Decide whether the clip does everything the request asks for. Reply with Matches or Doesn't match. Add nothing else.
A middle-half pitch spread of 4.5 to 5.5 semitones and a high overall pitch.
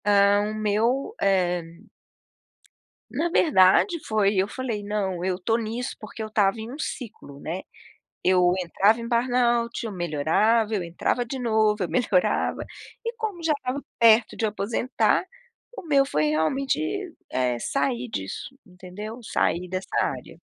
Matches